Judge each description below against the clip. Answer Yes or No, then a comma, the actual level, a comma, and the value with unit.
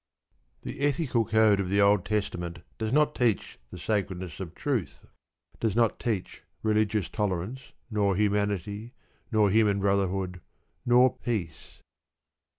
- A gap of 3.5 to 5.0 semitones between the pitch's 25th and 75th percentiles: No, narrow, 2.6 semitones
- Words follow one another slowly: Yes, slow, 125 wpm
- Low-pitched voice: Yes, low, 105 Hz